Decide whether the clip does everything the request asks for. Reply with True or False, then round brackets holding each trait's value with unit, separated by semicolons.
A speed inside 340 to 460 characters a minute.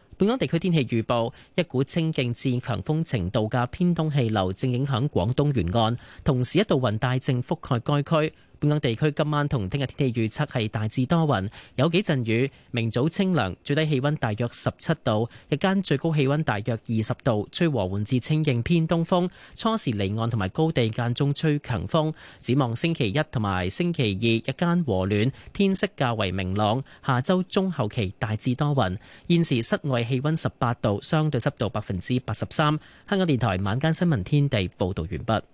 False (285 characters per minute)